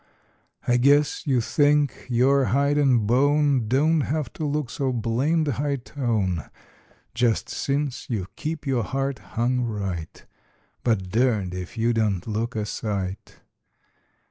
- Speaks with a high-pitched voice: No, low, 125 Hz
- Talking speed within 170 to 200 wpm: No, slow, 135 wpm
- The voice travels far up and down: No, average, 4.4 semitones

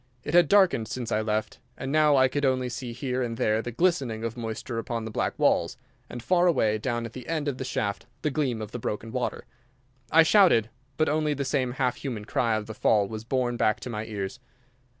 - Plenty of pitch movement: No, average, 4.0 semitones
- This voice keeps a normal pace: No, fast, 230 wpm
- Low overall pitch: Yes, low, 120 Hz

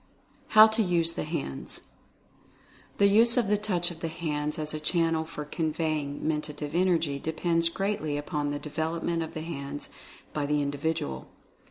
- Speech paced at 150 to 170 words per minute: Yes, average, 160 wpm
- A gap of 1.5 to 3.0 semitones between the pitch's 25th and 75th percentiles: Yes, narrow, 2.6 semitones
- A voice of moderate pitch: Yes, medium, 160 Hz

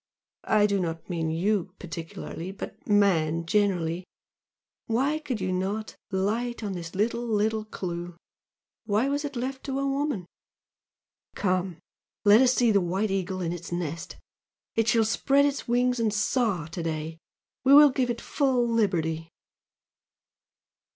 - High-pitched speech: Yes, high, 205 Hz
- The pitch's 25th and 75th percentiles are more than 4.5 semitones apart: Yes, wide, 5.5 semitones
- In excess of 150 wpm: No, average, 145 wpm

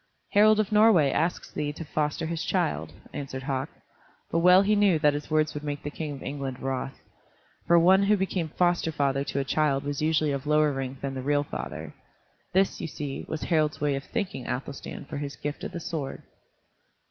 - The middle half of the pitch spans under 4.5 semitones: Yes, average, 3.5 semitones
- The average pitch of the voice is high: No, medium, 150 Hz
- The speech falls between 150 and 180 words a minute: No, fast, 205 wpm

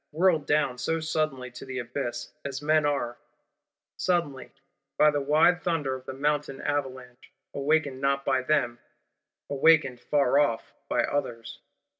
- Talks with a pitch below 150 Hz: Yes, medium, 140 Hz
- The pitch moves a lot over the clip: No, average, 2.7 semitones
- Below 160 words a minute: Yes, average, 140 wpm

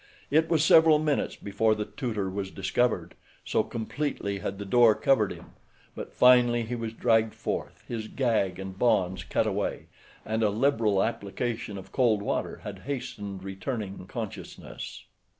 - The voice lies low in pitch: Yes, low, 110 Hz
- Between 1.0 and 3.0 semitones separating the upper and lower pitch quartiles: No, average, 3.8 semitones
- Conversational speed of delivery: Yes, average, 150 wpm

